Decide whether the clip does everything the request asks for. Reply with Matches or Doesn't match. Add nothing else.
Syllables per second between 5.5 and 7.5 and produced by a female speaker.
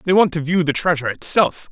Doesn't match